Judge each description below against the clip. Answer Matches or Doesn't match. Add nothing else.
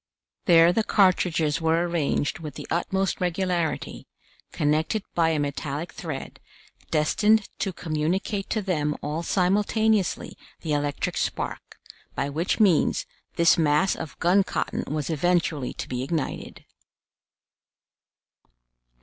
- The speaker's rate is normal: Doesn't match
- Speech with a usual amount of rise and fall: Matches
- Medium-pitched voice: Matches